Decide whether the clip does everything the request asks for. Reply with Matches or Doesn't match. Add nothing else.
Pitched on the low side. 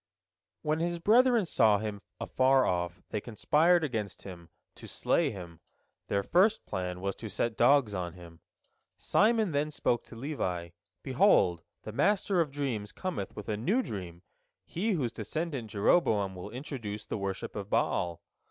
Matches